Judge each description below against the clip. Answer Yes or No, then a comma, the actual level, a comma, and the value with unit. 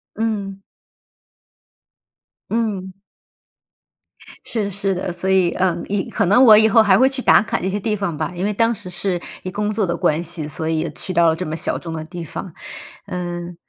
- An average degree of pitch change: Yes, average, 3.4 semitones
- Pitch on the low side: No, high, 190 Hz